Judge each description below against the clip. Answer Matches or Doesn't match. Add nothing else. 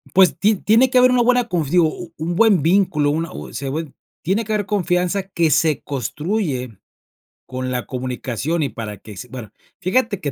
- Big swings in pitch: Matches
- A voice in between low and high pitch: Matches